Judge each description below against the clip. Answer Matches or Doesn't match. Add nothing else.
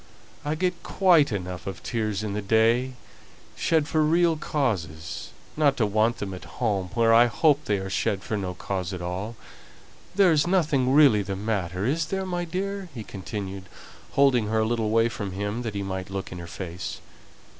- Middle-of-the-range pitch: Doesn't match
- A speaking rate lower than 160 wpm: Doesn't match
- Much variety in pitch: Matches